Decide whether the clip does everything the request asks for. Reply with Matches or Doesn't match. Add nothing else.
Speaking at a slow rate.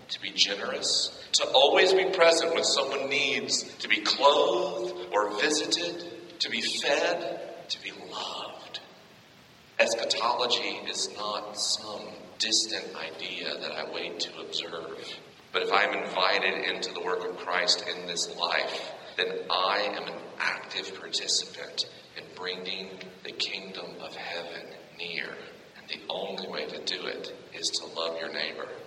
Doesn't match